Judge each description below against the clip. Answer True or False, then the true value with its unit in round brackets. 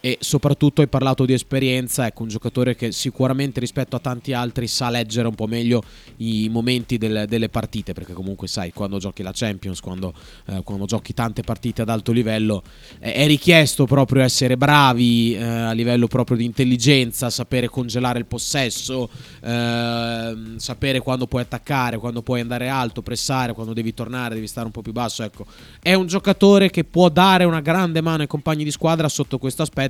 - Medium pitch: False (120 Hz)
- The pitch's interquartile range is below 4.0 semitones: True (2.8 semitones)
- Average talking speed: False (190 wpm)